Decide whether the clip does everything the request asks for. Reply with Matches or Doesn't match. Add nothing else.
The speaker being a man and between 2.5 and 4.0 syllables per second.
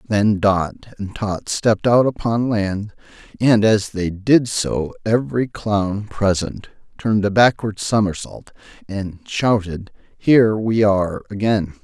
Matches